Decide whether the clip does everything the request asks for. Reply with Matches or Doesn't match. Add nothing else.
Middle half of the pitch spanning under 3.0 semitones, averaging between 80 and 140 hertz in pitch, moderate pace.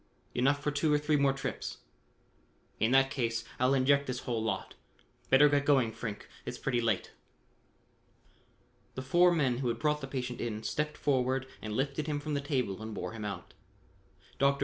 Doesn't match